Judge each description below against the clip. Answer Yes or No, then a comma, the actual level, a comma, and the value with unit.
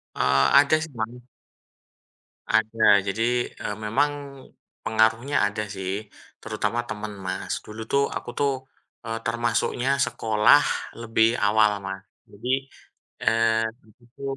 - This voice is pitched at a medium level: No, low, 110 Hz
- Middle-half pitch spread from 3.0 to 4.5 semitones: No, narrow, 2.4 semitones